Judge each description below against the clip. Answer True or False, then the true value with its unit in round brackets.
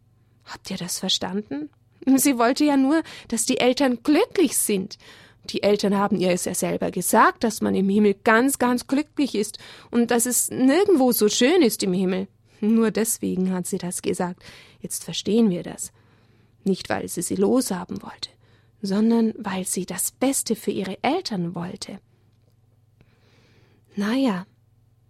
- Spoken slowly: False (155 wpm)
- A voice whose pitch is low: False (200 Hz)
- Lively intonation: True (5.9 semitones)